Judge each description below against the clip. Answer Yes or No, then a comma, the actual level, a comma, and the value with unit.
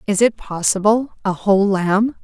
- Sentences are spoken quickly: No, average, 160 wpm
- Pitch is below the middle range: No, high, 205 Hz